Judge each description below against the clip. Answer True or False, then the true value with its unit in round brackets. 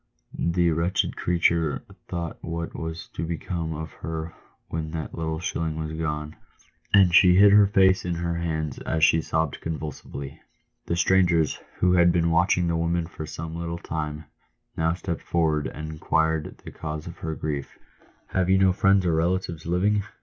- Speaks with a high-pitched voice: False (85 Hz)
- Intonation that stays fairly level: True (1.8 semitones)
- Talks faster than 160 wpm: True (170 wpm)